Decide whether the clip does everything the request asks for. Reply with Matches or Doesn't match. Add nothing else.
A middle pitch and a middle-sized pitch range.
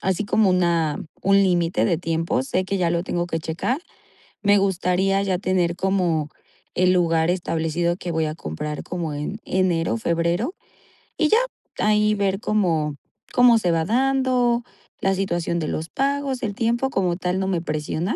Matches